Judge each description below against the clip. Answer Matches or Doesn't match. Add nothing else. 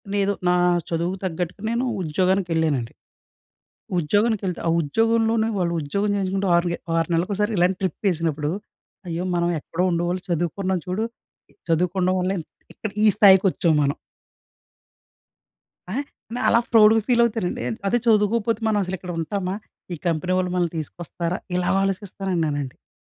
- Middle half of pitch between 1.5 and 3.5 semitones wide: Matches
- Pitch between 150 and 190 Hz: Matches